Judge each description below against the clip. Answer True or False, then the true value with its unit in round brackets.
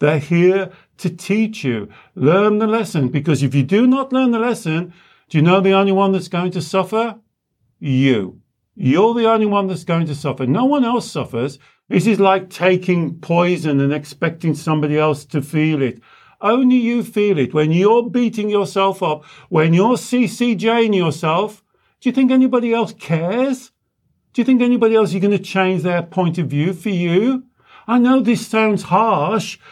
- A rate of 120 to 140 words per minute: False (180 wpm)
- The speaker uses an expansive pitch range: True (5.9 semitones)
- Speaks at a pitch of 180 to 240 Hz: True (190 Hz)